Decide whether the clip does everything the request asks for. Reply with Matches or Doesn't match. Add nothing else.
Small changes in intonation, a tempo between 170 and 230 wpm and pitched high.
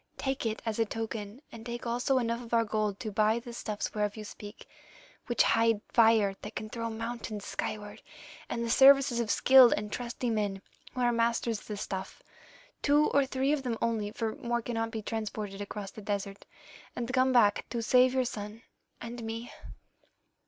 Matches